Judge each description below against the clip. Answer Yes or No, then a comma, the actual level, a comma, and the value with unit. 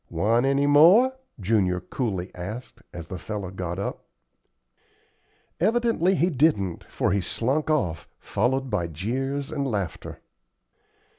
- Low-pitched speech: Yes, low, 115 Hz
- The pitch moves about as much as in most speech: No, wide, 7.5 semitones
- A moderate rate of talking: No, slow, 125 wpm